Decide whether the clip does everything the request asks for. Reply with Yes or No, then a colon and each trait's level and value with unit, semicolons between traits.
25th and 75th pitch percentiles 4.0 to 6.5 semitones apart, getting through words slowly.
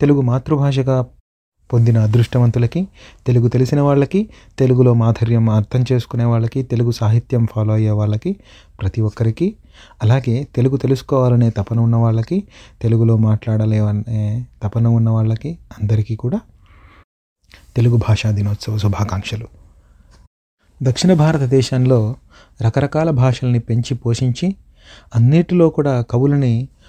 No: average, 3.0 semitones; slow, 100 wpm